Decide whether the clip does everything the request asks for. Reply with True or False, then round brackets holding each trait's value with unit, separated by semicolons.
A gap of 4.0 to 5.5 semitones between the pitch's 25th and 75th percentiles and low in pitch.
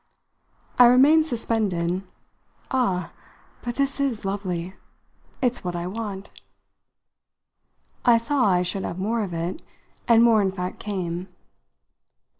False (4.9 semitones; 205 Hz)